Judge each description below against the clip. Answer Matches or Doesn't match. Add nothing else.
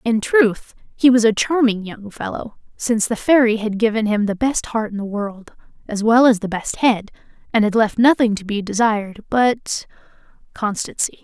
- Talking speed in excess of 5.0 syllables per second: Doesn't match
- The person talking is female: Matches